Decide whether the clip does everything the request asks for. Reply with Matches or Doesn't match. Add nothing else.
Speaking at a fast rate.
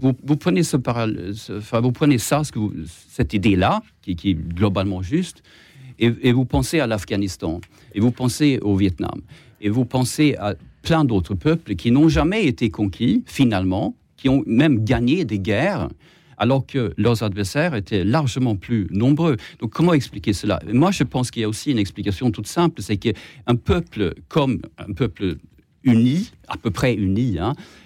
Doesn't match